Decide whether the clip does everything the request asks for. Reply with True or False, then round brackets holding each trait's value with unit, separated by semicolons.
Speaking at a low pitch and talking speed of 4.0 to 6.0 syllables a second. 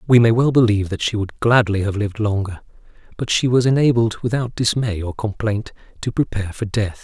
True (110 Hz; 5.8 syllables/s)